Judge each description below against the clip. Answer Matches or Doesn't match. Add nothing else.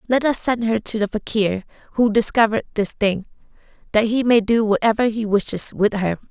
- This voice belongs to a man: Doesn't match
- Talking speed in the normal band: Matches